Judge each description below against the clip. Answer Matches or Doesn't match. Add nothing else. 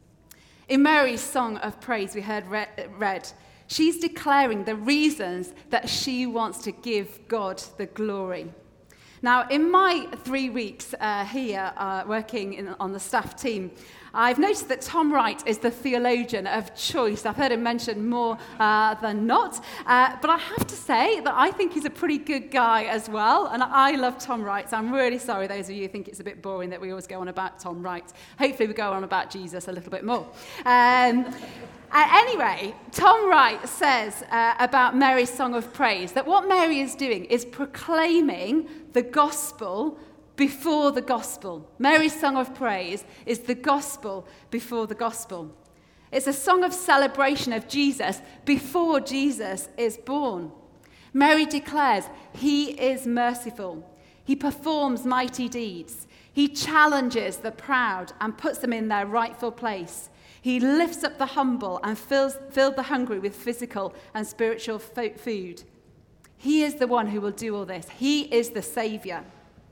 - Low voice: Doesn't match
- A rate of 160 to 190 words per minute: Matches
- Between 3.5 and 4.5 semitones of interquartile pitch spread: Doesn't match